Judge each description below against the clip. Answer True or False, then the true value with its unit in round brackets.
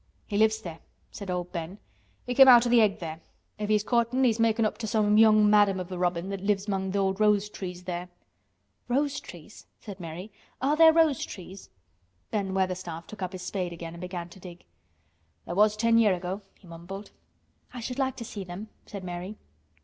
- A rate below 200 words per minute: False (205 wpm)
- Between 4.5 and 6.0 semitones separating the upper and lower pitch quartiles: False (3.4 semitones)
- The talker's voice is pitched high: True (200 Hz)